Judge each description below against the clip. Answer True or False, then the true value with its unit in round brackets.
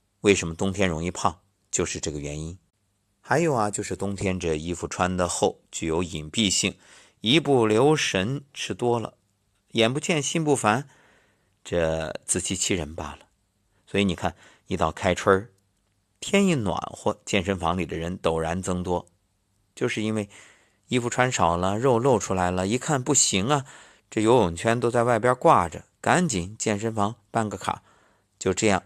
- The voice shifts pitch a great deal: False (4.0 semitones)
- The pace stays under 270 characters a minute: True (235 characters per minute)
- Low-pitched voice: True (100 Hz)